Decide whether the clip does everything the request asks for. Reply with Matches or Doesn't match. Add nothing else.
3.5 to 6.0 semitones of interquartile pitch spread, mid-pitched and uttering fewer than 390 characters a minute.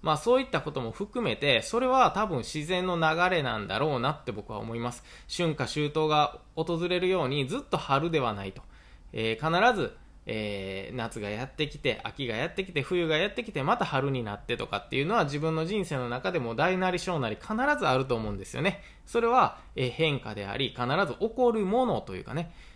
Doesn't match